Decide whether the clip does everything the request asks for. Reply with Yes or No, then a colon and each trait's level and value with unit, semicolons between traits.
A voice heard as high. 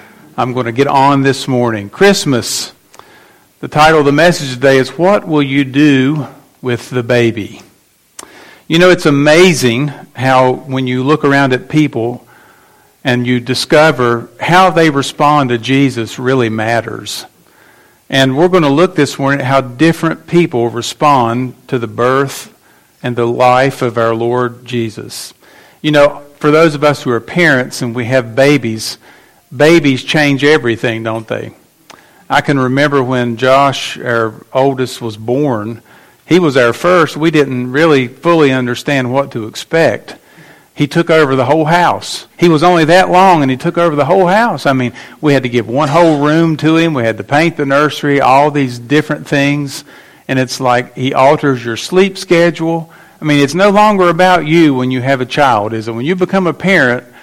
No: medium, 140 Hz